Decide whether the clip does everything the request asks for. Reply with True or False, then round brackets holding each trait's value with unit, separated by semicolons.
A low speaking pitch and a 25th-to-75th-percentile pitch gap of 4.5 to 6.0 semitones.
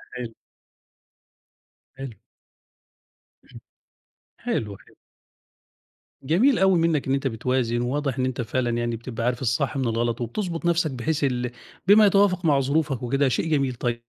True (130 Hz; 5.0 semitones)